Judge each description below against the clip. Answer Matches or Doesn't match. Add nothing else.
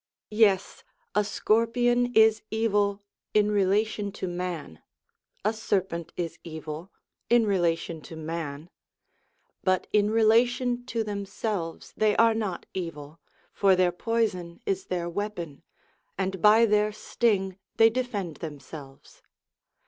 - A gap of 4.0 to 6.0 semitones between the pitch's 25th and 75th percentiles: Matches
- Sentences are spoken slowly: Matches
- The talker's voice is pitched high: Matches